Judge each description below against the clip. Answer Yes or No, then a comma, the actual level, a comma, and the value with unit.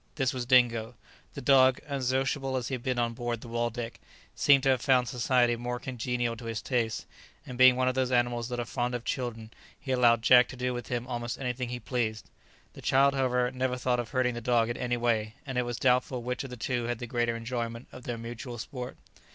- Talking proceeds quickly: Yes, fast, 230 wpm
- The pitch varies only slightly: Yes, narrow, 1.3 semitones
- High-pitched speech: No, low, 125 Hz